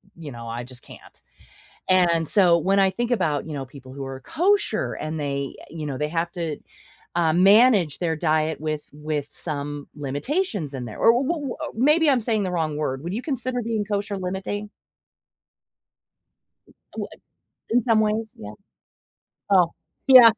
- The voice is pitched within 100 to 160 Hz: No, medium, 170 Hz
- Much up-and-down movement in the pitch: Yes, wide, 6.6 semitones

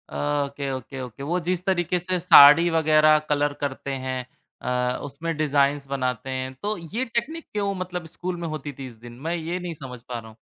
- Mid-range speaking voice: Yes, medium, 150 Hz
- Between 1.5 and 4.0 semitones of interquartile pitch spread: No, average, 4.5 semitones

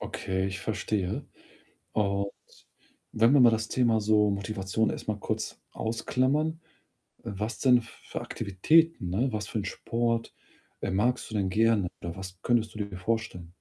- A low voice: Yes, low, 110 Hz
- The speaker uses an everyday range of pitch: Yes, average, 3.1 semitones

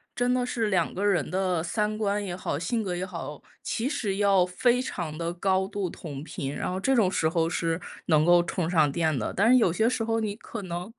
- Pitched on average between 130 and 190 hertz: Yes, medium, 185 Hz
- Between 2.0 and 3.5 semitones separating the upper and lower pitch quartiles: No, average, 4.1 semitones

